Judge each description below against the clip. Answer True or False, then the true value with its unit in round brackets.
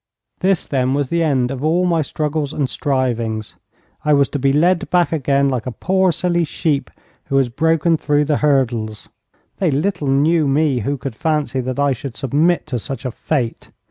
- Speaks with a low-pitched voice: False (145 Hz)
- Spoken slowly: False (190 wpm)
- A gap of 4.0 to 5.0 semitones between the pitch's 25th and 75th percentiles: False (3.5 semitones)